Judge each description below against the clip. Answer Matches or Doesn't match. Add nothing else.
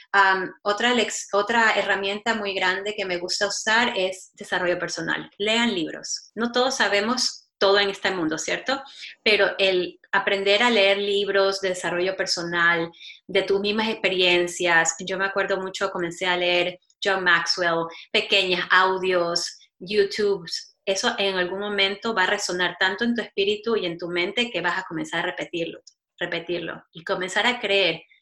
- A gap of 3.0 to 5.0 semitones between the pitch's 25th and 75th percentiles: Doesn't match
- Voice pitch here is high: Matches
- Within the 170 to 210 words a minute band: Doesn't match